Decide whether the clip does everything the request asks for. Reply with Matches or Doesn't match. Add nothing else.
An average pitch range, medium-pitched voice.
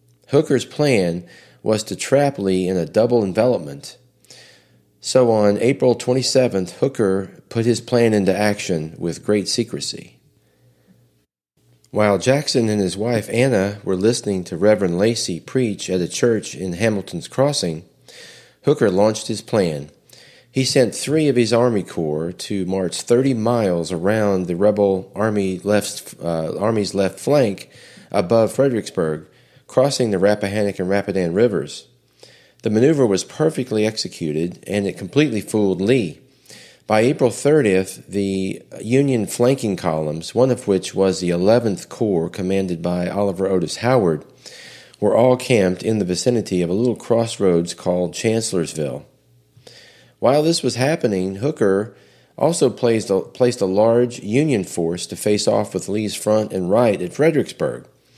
Doesn't match